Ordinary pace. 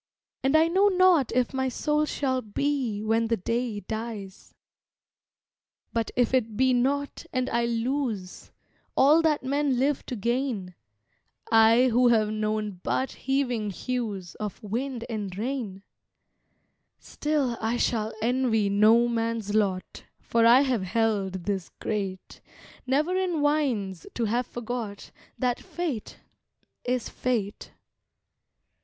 No: slow, 125 wpm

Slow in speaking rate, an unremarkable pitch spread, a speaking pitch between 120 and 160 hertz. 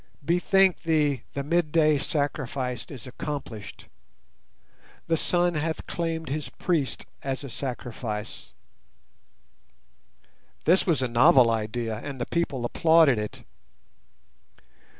Yes: slow, 105 wpm; average, 4.9 semitones; medium, 140 Hz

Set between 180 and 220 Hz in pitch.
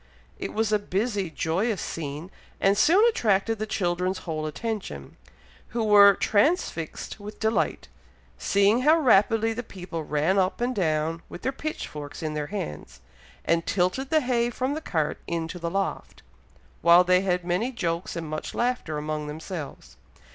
Yes: high, 190 Hz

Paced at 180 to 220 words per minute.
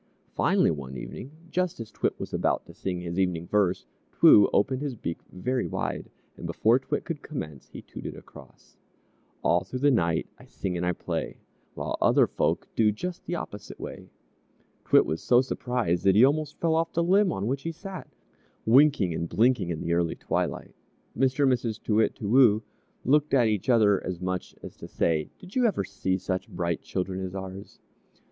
Yes: average, 195 wpm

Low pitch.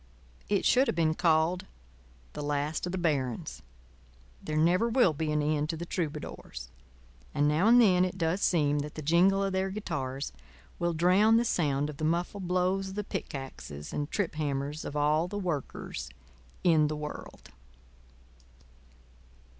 No: medium, 160 Hz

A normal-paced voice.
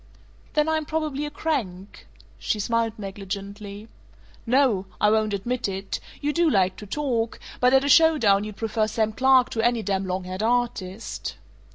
Yes: average, 170 wpm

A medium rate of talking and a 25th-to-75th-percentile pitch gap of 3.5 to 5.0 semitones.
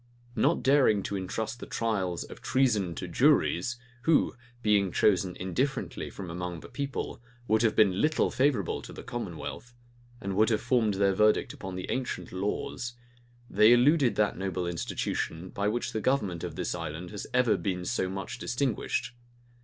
Yes: average, 165 wpm; average, 4.7 semitones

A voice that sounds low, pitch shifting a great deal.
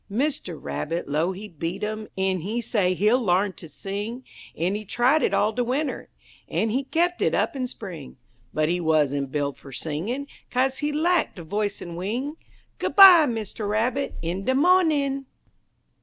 No: high, 215 Hz; wide, 7.2 semitones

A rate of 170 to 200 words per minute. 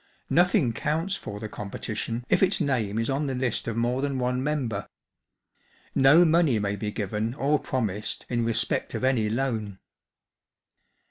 No: average, 155 wpm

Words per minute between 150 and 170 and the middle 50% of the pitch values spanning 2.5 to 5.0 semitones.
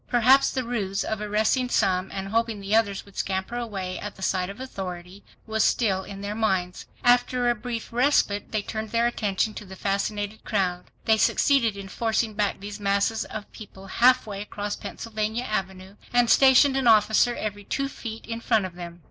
No: average, 190 wpm; average, 3.0 semitones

